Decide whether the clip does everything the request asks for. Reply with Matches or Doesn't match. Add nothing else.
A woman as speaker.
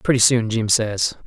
Doesn't match